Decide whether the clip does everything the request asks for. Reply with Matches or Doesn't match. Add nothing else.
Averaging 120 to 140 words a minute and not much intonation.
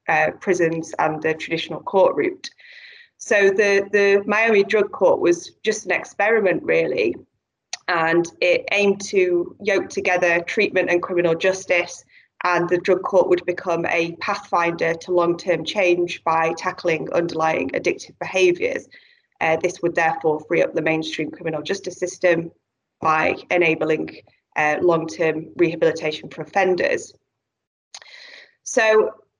Doesn't match